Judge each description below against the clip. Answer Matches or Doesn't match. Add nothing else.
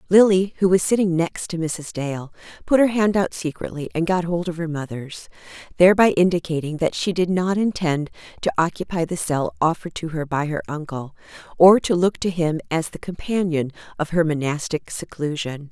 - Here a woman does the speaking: Matches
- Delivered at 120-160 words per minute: Doesn't match